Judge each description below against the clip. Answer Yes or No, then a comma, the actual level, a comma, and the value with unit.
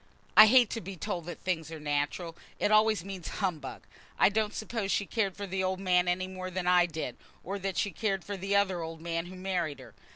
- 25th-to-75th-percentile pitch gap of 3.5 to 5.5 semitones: No, average, 2.7 semitones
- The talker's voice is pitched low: No, medium, 185 Hz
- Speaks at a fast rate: Yes, fast, 230 wpm